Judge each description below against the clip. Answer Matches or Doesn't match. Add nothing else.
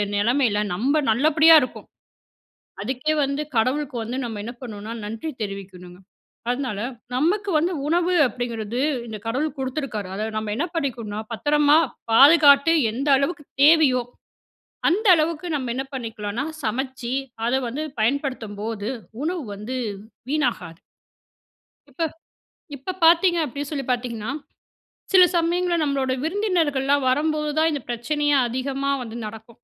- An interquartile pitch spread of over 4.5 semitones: Matches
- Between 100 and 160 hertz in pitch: Doesn't match